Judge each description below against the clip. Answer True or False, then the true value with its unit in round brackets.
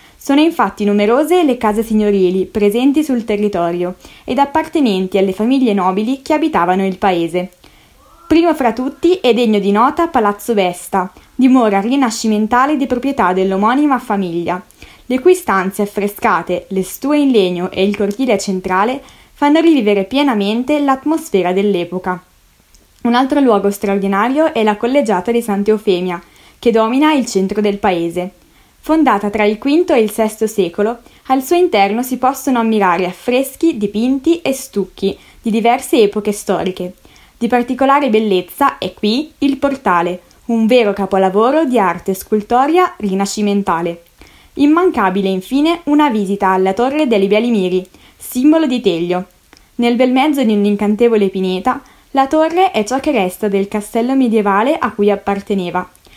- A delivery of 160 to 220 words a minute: False (140 wpm)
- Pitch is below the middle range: False (215 Hz)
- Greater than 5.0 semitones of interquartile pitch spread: True (5.5 semitones)